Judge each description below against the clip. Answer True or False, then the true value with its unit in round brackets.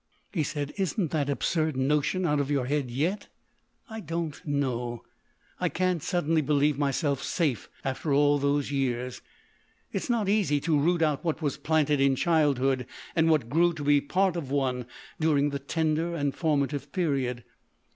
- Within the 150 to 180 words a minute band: True (165 wpm)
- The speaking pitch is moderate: True (145 Hz)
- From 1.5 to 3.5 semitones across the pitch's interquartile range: True (3.0 semitones)